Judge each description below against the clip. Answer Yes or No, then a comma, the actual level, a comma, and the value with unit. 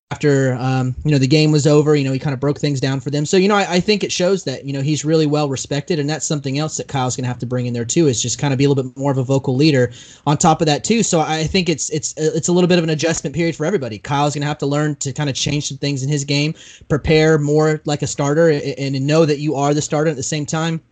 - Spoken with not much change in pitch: Yes, narrow, 2.3 semitones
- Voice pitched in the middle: Yes, medium, 150 Hz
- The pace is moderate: No, fast, 315 wpm